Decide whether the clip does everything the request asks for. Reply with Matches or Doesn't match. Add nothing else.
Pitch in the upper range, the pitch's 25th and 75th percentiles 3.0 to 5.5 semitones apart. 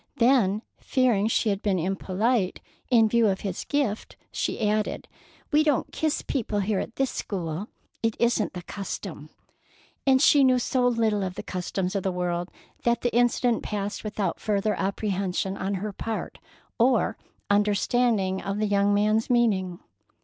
Matches